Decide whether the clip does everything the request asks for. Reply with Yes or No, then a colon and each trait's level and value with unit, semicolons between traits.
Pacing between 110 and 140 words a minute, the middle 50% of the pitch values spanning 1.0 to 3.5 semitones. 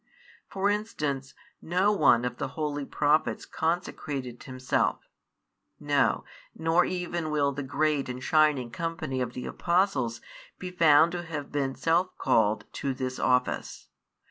No: slow, 135 wpm; average, 4.4 semitones